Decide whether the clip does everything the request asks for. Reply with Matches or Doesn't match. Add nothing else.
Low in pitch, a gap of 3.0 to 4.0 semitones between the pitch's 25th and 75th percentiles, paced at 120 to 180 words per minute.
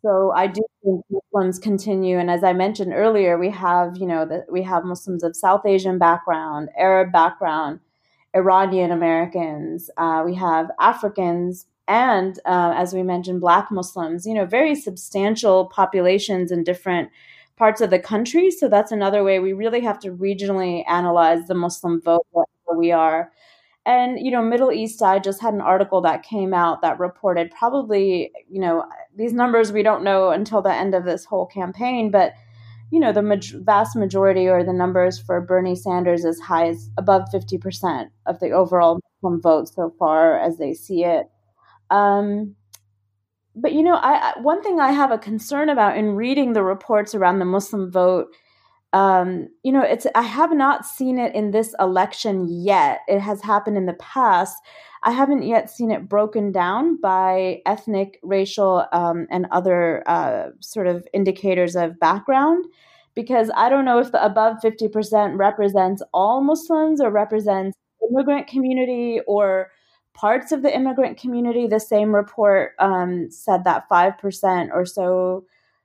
Doesn't match